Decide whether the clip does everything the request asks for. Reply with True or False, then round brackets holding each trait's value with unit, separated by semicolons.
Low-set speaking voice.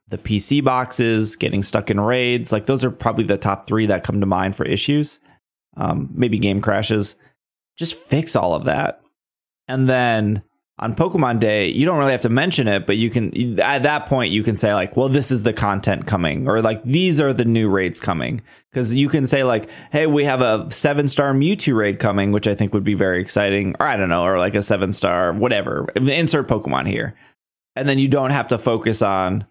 True (115 Hz)